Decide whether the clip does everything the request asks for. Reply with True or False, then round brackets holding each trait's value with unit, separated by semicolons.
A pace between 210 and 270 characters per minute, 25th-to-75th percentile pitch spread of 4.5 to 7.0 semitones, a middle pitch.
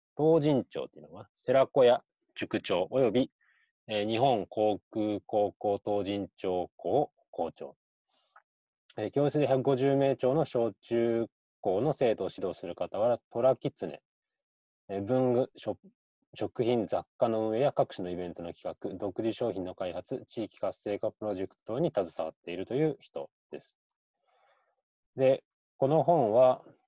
False (255 characters per minute; 5.1 semitones; 115 Hz)